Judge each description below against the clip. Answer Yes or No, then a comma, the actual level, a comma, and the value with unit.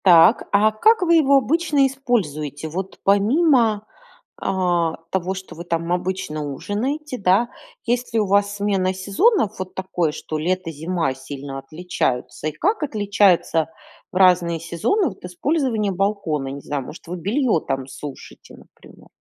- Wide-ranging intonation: Yes, wide, 5.7 semitones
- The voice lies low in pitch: No, high, 190 Hz